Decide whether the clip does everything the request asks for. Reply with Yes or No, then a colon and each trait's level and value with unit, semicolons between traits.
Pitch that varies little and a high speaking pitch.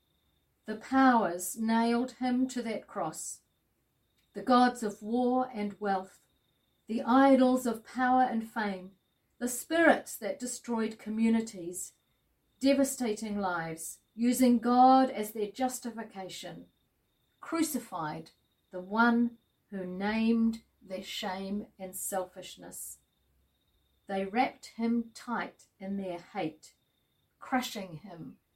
No: average, 4.7 semitones; high, 225 Hz